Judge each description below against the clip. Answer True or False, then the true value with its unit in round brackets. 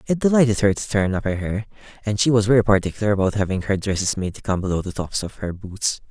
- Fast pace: True (255 wpm)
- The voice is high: False (100 Hz)